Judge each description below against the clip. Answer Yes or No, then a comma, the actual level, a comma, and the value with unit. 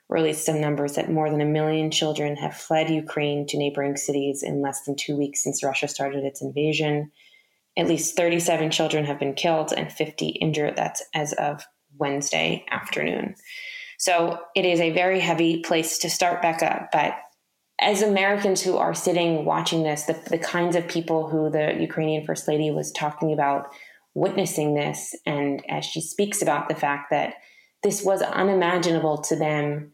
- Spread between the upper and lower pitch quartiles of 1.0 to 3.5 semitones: Yes, narrow, 2.6 semitones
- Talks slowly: No, average, 175 wpm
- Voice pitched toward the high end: No, medium, 155 Hz